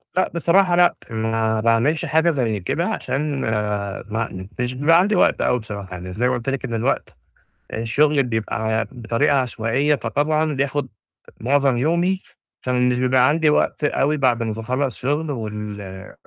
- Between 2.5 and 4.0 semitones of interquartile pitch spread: No, average, 4.8 semitones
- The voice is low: Yes, low, 125 Hz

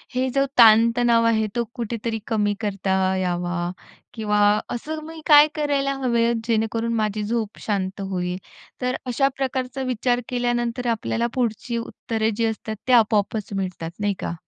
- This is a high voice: Yes, high, 230 Hz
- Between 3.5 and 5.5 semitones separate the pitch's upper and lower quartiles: No, average, 3.0 semitones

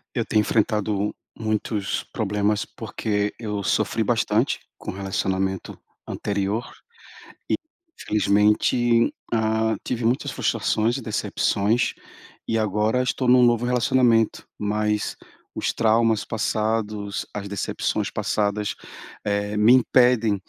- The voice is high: No, low, 110 Hz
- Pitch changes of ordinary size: No, narrow, 1.9 semitones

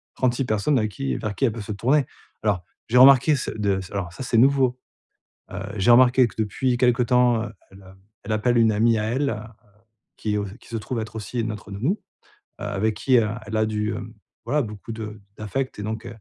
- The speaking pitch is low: Yes, low, 110 Hz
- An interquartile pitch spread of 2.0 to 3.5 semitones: Yes, average, 2.9 semitones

